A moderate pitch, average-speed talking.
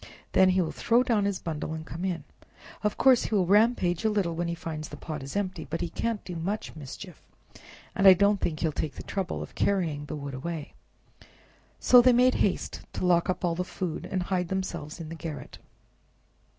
No: medium, 180 Hz; fast, 215 wpm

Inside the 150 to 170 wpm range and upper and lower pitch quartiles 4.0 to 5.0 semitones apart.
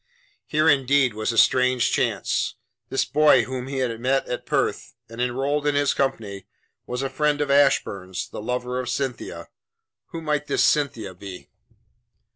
No: average, 160 wpm; average, 3.0 semitones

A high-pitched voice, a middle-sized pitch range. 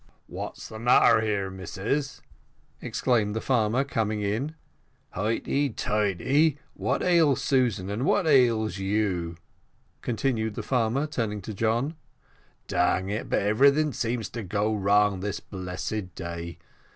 No: low, 110 Hz; average, 4.2 semitones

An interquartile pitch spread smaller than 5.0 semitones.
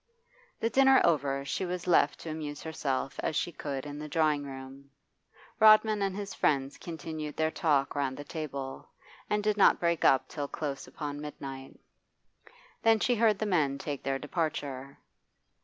Yes: average, 4.2 semitones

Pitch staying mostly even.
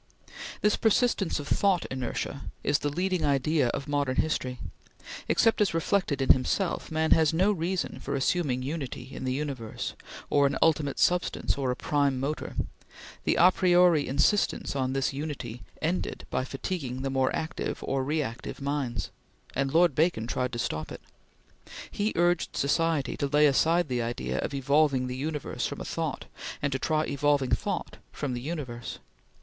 No: average, 3.9 semitones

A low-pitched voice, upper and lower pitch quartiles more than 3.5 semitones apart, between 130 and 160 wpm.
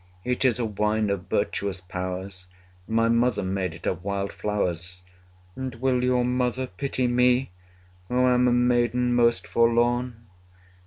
Yes: low, 115 Hz; average, 3.9 semitones; average, 145 wpm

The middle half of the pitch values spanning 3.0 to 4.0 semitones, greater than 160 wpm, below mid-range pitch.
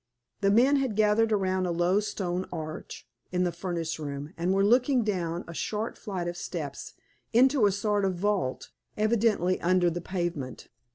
No: average, 3.4 semitones; average, 170 wpm; medium, 185 Hz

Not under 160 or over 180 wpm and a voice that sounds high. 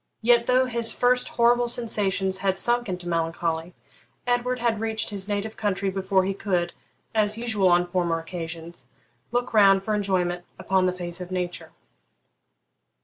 No: average, 150 wpm; high, 195 Hz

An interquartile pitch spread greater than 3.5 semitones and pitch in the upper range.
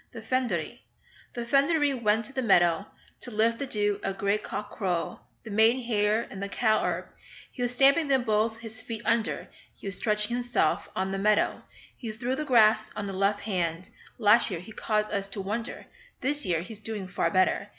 No: average, 3.2 semitones; high, 215 Hz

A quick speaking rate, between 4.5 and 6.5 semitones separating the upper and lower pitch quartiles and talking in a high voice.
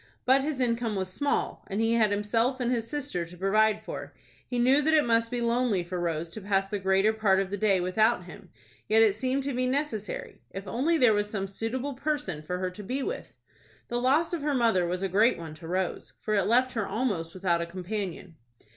Yes: fast, 225 wpm; average, 4.9 semitones; high, 215 Hz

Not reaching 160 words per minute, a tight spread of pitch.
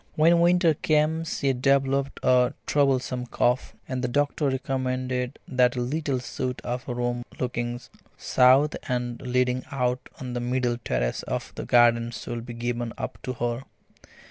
Yes: average, 150 wpm; narrow, 2.0 semitones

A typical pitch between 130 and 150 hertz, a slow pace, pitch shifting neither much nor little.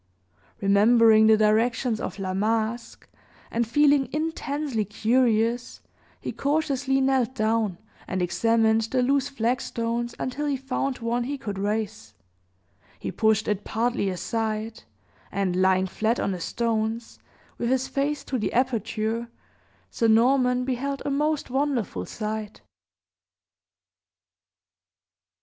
No: high, 230 Hz; slow, 120 wpm; average, 3.3 semitones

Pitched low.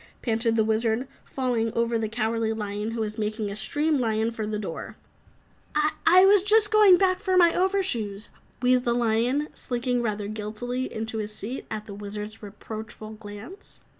No: high, 225 Hz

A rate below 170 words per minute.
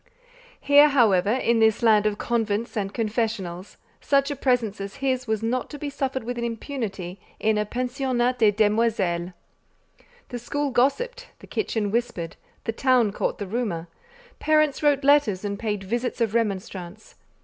Yes: average, 155 wpm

